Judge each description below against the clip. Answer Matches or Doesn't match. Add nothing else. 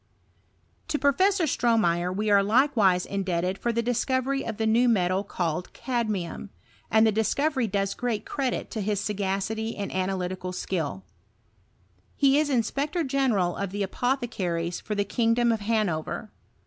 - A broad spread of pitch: Doesn't match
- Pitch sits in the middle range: Doesn't match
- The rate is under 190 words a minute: Matches